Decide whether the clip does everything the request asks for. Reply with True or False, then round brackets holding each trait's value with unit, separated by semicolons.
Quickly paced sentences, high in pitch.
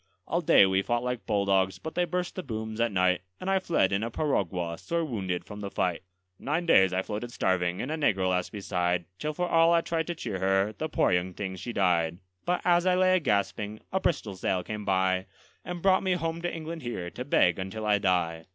False (230 wpm; 105 Hz)